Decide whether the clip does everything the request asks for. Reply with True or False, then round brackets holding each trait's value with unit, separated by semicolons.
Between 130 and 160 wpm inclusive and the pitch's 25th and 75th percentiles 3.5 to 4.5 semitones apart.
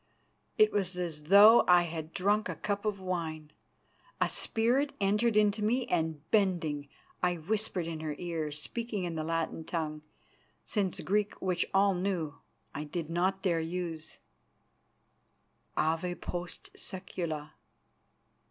True (135 wpm; 4.0 semitones)